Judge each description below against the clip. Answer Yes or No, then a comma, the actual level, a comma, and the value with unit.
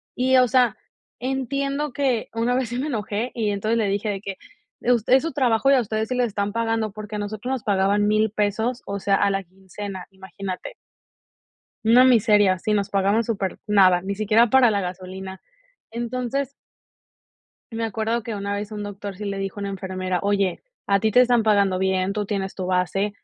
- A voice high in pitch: Yes, high, 210 Hz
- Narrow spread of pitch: No, average, 3.2 semitones